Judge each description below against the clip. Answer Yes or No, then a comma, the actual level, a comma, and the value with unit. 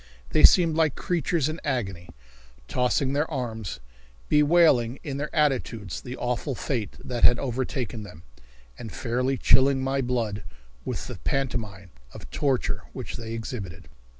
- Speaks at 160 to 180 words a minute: No, average, 140 wpm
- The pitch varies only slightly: No, average, 3.6 semitones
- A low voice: Yes, low, 125 Hz